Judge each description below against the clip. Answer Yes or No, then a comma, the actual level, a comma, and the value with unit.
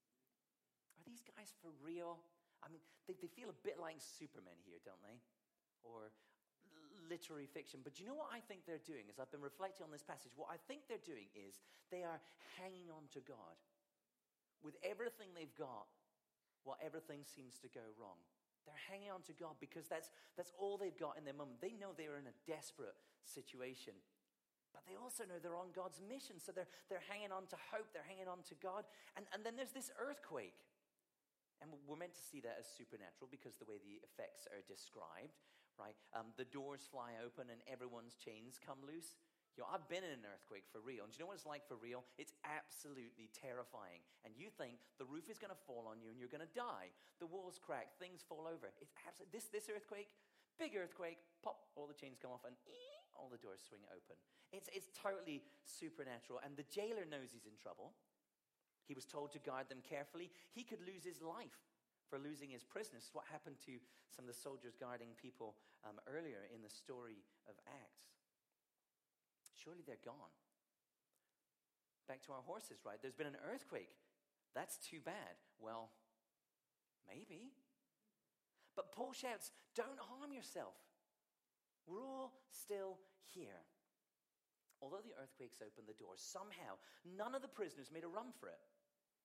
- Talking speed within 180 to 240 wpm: Yes, average, 185 wpm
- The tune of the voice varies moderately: No, wide, 7.4 semitones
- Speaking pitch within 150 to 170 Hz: Yes, medium, 165 Hz